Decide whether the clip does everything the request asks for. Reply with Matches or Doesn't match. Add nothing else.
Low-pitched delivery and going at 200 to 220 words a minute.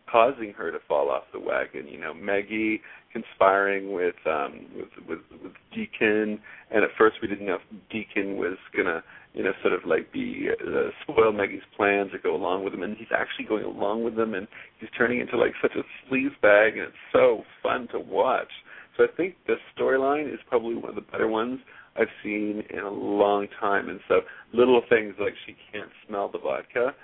Matches